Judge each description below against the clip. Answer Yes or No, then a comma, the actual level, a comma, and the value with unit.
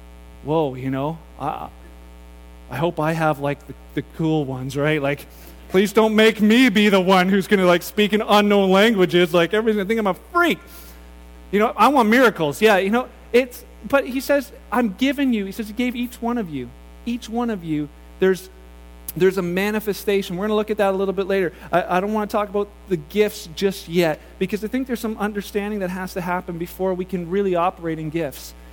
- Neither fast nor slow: No, fast, 215 wpm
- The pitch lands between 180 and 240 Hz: Yes, high, 190 Hz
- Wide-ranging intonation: Yes, wide, 5.9 semitones